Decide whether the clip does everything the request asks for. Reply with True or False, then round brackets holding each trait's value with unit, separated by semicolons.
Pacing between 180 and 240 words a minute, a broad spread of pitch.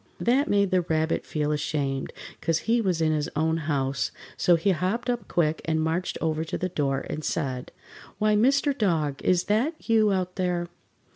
False (185 wpm; 4.8 semitones)